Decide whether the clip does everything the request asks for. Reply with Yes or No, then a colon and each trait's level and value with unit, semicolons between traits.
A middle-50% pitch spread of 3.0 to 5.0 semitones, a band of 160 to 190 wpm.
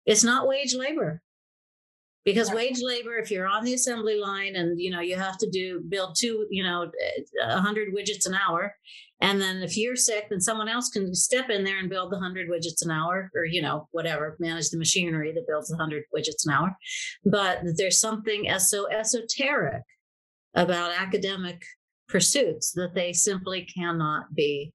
Yes: average, 4.1 semitones; average, 180 wpm